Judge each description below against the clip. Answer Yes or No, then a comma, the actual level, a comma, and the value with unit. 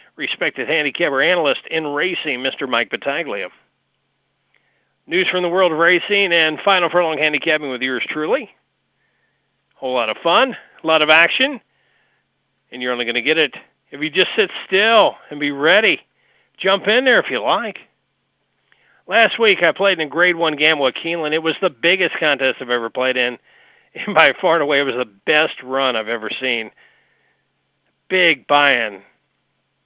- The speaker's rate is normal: Yes, average, 175 wpm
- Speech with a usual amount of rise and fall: Yes, average, 4.9 semitones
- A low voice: No, medium, 160 Hz